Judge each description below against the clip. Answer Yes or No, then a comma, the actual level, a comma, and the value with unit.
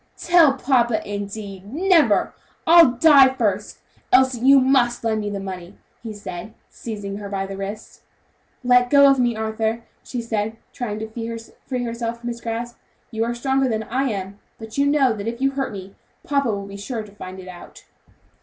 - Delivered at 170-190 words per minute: Yes, average, 180 wpm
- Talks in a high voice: Yes, high, 230 Hz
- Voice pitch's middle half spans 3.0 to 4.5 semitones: Yes, average, 4.0 semitones